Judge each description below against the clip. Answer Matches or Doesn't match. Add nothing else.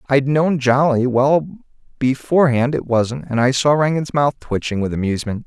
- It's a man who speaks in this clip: Matches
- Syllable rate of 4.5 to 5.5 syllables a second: Matches